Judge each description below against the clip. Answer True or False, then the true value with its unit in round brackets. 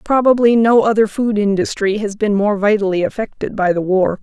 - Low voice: False (210 Hz)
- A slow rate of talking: False (185 wpm)